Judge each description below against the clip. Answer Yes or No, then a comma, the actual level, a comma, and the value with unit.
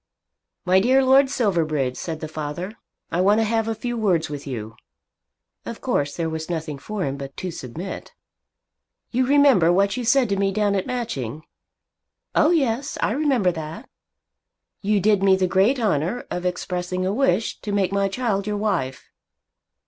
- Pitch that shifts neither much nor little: No, wide, 5.7 semitones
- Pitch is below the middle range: No, high, 195 Hz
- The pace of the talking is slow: No, average, 170 wpm